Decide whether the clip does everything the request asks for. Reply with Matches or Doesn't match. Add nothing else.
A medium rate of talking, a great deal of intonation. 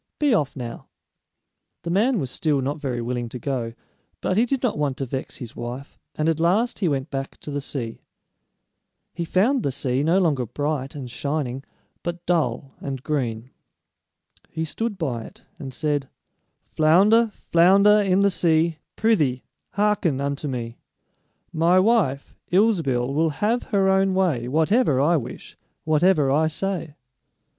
Matches